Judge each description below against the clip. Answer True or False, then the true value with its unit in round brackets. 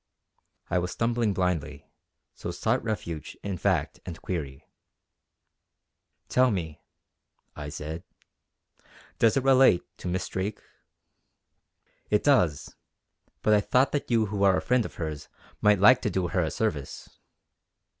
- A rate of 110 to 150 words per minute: True (135 wpm)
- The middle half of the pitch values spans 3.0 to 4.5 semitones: False (5.3 semitones)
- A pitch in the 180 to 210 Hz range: False (95 Hz)